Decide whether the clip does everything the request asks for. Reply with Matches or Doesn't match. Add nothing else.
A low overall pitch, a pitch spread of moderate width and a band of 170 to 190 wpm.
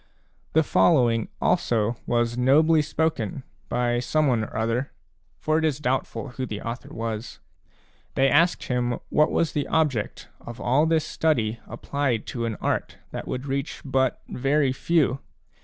Doesn't match